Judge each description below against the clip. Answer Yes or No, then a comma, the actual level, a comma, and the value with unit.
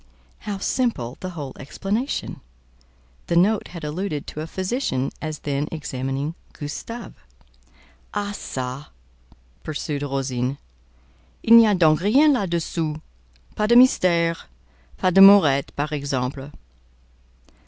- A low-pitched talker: No, medium, 160 Hz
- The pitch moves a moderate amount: No, wide, 6.1 semitones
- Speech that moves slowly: Yes, slow, 115 wpm